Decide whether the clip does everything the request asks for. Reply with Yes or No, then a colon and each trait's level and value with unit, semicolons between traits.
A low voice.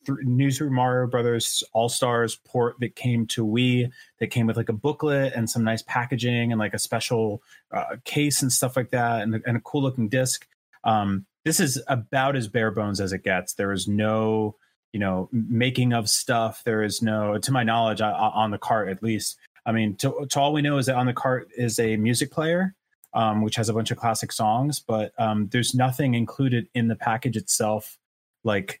Yes: low, 115 Hz